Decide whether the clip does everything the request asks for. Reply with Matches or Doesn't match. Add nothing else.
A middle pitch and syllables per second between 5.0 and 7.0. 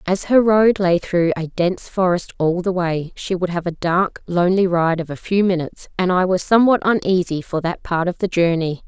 Matches